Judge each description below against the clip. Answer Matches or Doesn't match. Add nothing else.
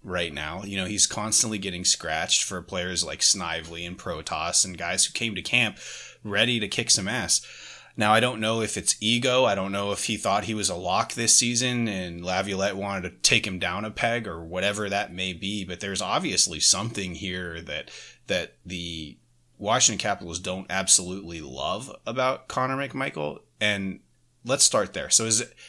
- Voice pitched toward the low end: Matches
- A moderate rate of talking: Matches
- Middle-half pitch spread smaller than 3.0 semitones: Doesn't match